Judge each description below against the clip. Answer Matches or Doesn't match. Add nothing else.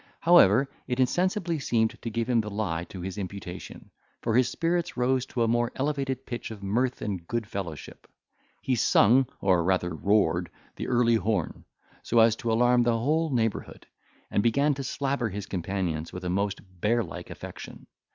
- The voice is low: Matches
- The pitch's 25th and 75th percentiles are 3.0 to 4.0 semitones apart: Doesn't match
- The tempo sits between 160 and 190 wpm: Matches